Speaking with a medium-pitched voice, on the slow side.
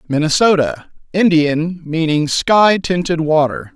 Yes: medium, 165 Hz; slow, 80 wpm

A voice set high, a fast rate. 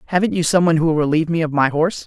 No: medium, 160 Hz; fast, 320 wpm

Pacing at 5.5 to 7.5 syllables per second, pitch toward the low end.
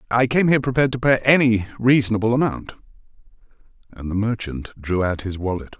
Yes: 6.2 syllables/s; low, 115 Hz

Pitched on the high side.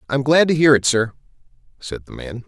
No: low, 135 Hz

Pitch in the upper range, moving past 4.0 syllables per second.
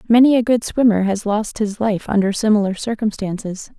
Yes: high, 215 Hz; 5.3 syllables/s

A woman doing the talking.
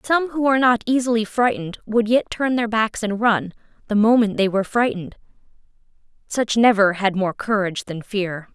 Yes: female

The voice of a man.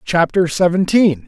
Yes: male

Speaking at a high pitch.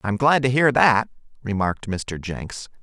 No: low, 115 Hz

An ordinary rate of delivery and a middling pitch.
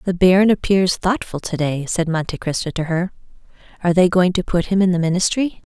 No: fast, 210 wpm; medium, 180 Hz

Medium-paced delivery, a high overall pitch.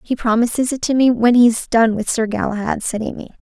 No: fast, 240 wpm; high, 230 Hz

